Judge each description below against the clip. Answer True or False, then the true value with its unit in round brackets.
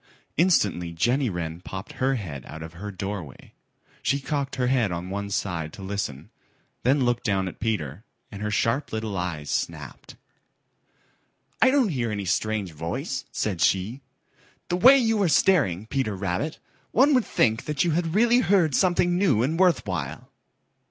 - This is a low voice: True (110 Hz)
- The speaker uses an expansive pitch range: True (8.7 semitones)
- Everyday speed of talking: True (165 wpm)